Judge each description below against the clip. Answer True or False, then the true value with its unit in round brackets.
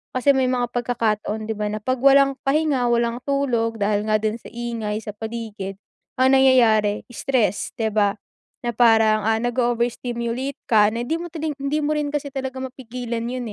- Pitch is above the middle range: True (240 Hz)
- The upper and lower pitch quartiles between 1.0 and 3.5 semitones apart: True (3.2 semitones)